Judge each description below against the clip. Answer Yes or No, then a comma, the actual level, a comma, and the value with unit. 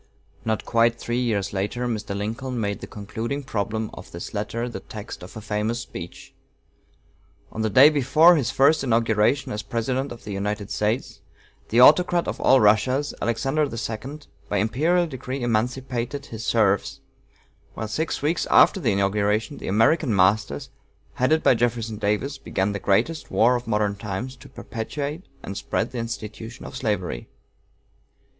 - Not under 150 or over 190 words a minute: Yes, average, 160 wpm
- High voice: No, low, 115 Hz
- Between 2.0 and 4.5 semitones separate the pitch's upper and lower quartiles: Yes, average, 3.8 semitones